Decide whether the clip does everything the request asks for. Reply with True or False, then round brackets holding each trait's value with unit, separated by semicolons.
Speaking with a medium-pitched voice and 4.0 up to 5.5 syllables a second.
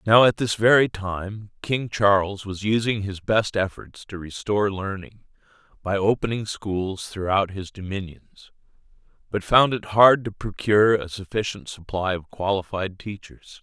False (100 Hz; 4.4 syllables/s)